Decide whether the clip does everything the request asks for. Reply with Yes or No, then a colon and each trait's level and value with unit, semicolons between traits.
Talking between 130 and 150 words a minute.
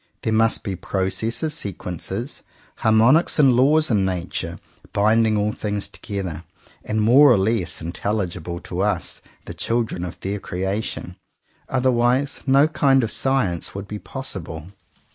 Yes: slow, 135 wpm